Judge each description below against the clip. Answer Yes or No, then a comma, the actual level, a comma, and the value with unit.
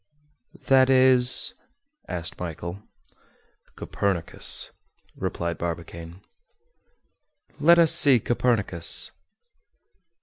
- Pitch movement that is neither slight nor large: No, wide, 7.4 semitones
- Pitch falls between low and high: No, low, 100 Hz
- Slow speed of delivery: Yes, slow, 65 wpm